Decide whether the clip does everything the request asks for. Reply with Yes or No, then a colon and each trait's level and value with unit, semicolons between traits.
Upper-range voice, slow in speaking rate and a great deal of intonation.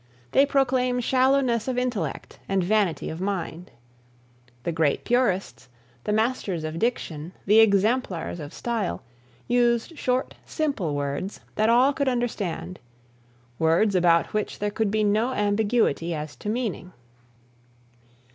Yes: high, 210 Hz; slow, 130 wpm; wide, 6.0 semitones